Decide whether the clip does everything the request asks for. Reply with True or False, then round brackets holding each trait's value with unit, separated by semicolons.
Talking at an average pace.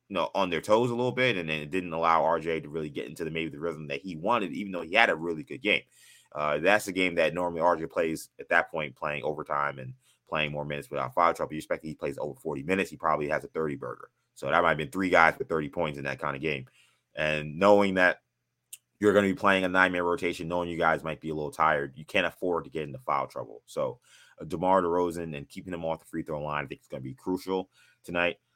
False (270 wpm)